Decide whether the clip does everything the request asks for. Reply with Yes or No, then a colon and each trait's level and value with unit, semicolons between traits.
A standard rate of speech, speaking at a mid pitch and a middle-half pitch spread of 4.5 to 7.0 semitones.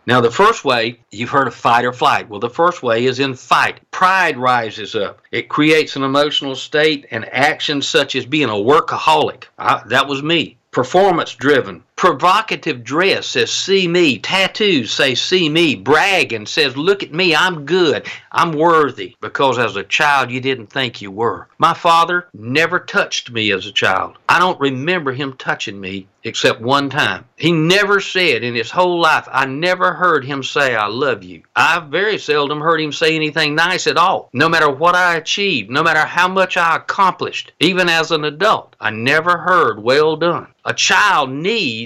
Yes: average, 185 wpm; medium, 150 Hz; average, 4.8 semitones